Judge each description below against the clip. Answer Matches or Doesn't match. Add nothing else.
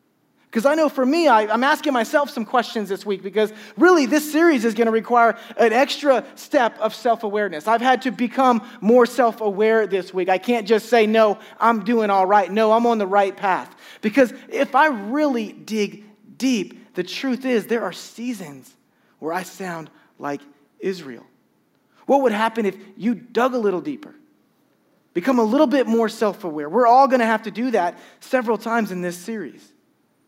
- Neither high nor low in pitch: Doesn't match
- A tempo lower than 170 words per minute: Doesn't match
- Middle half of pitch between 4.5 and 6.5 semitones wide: Doesn't match